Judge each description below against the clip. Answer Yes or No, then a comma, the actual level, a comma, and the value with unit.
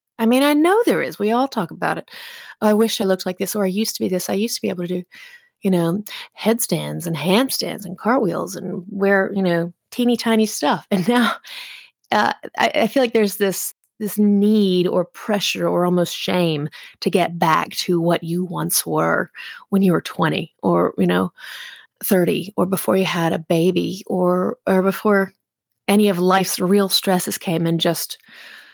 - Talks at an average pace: Yes, average, 195 wpm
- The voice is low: No, high, 195 Hz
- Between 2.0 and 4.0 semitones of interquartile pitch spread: Yes, average, 3.4 semitones